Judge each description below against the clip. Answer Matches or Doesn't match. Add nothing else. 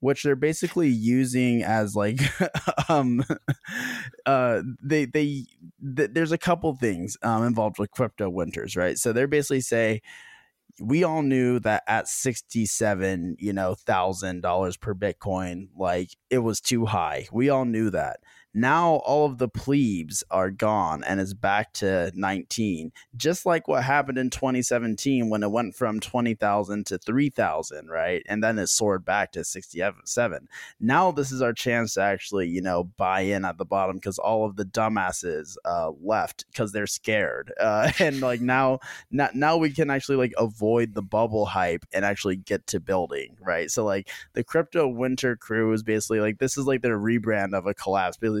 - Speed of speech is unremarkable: Matches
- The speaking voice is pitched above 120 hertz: Doesn't match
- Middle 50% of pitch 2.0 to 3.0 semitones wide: Doesn't match